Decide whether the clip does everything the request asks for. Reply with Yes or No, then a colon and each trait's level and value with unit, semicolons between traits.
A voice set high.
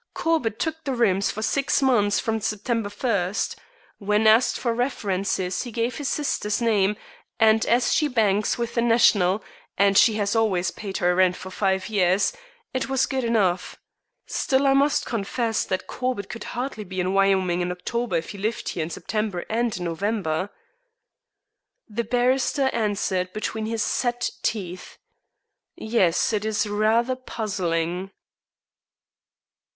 Yes: high, 215 Hz